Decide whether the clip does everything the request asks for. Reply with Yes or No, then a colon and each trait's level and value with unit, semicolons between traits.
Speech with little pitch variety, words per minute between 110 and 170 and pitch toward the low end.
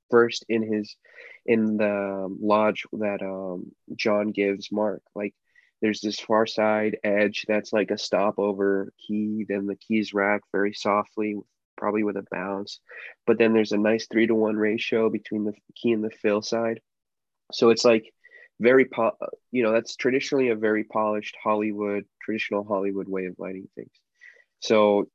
Yes: narrow, 1.7 semitones; average, 160 wpm; low, 105 Hz